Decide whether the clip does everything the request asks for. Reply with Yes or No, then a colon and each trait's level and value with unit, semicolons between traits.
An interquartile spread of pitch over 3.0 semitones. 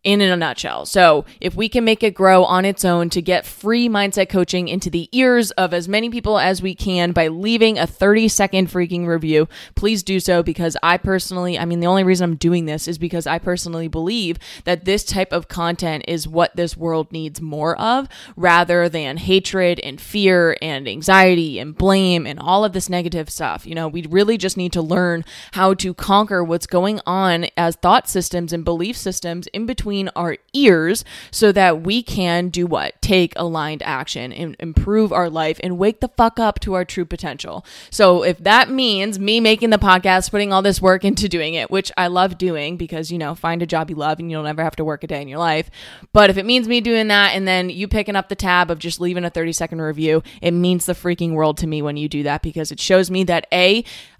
No: narrow, 2.5 semitones